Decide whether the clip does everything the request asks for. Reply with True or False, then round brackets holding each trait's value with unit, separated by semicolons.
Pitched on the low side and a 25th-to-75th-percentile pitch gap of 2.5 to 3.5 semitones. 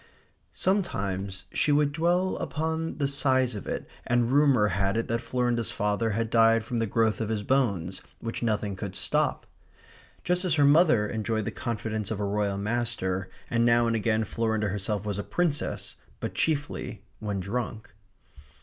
False (115 Hz; 4.3 semitones)